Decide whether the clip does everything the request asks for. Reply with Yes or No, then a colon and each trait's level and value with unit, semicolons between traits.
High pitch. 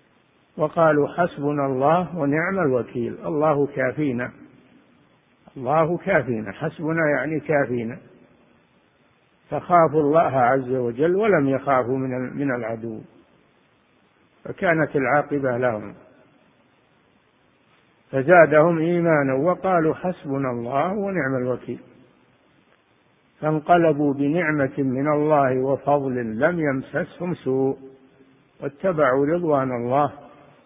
No: medium, 145 Hz